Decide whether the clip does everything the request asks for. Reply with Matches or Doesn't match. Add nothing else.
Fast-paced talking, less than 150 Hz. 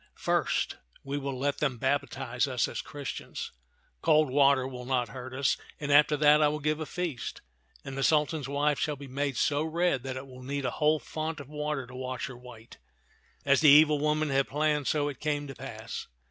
Matches